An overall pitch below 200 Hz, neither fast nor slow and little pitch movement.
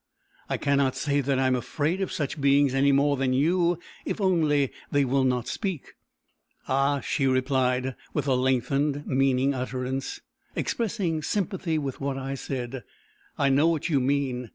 Yes: medium, 140 Hz; average, 160 wpm; narrow, 2.0 semitones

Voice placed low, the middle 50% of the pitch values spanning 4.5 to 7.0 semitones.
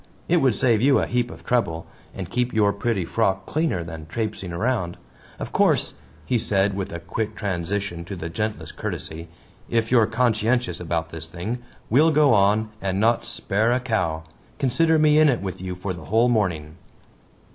Yes: low, 105 Hz; average, 5.3 semitones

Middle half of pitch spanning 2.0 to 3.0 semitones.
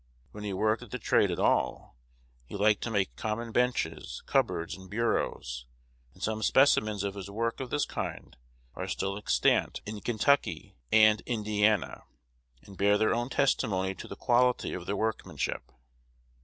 Yes: average, 2.7 semitones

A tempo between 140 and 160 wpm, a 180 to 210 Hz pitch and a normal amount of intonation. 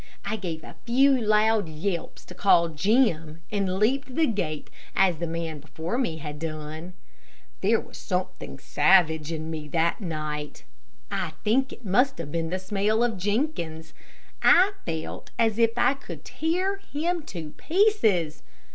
No: average, 155 wpm; medium, 185 Hz; wide, 6.7 semitones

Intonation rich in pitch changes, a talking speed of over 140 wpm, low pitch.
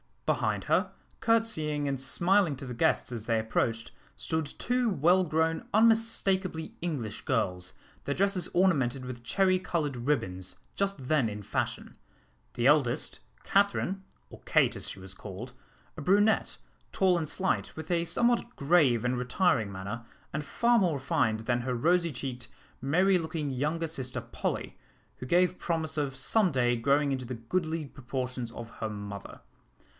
No: wide, 6.6 semitones; average, 155 wpm; medium, 145 Hz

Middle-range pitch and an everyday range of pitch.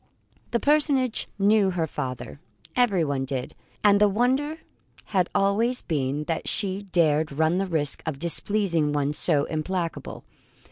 No: medium, 180 Hz; wide, 5.7 semitones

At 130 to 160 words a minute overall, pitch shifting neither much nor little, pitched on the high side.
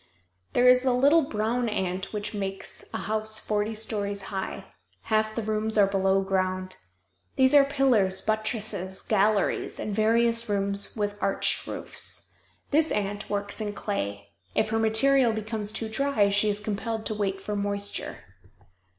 No: average, 150 wpm; narrow, 1.9 semitones; high, 215 Hz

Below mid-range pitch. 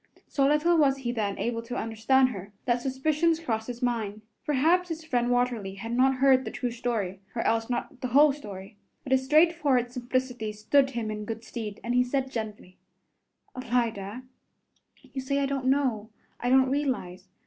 No: high, 245 Hz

